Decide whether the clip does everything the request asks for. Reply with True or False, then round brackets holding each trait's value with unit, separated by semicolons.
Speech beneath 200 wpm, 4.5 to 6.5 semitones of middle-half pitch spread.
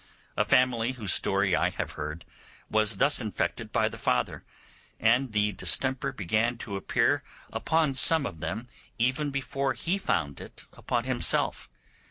True (150 wpm; 4.9 semitones)